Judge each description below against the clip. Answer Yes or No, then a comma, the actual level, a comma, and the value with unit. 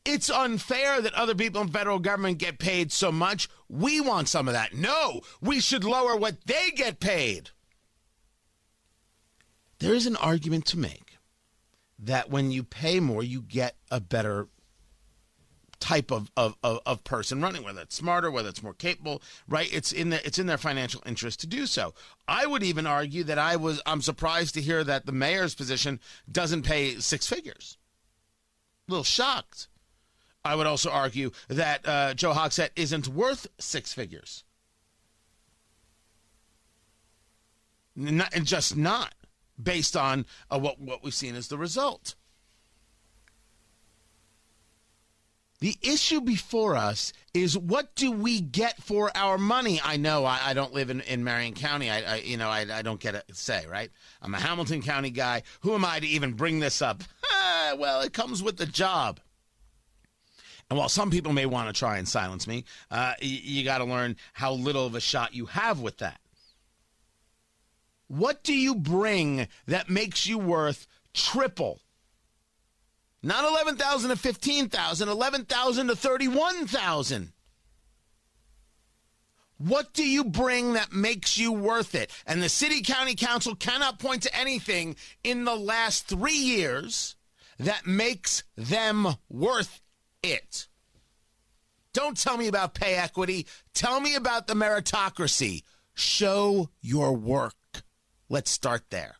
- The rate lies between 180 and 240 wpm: No, average, 150 wpm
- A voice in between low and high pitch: Yes, medium, 155 Hz